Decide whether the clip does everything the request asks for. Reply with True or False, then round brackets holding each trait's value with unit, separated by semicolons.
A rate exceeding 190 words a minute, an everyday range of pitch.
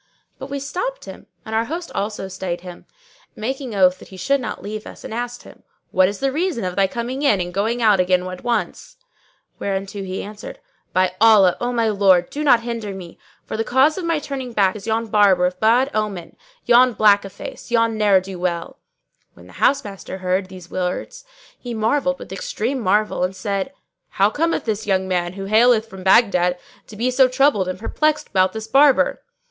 True (200 wpm; 4.7 semitones)